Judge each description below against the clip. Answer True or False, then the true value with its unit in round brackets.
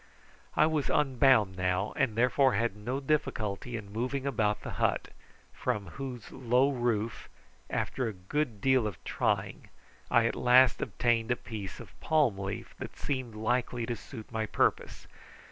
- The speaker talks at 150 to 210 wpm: True (155 wpm)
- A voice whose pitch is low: True (120 Hz)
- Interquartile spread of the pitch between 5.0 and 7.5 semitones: False (3.7 semitones)